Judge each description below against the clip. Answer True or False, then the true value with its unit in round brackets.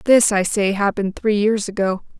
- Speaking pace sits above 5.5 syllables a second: False (5.2 syllables/s)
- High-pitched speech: True (205 Hz)